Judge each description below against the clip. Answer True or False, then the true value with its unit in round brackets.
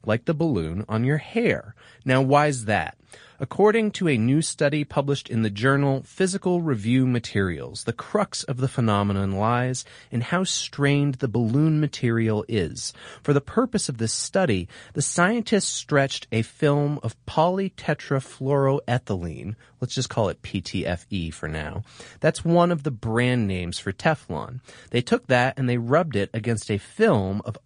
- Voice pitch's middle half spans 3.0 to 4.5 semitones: False (5.2 semitones)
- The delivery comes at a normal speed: True (160 wpm)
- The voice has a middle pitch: False (125 Hz)